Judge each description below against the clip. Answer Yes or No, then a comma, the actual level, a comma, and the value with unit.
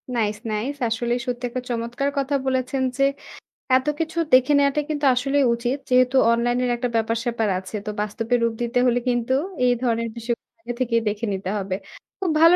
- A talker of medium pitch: No, high, 245 Hz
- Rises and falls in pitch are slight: Yes, narrow, 2.2 semitones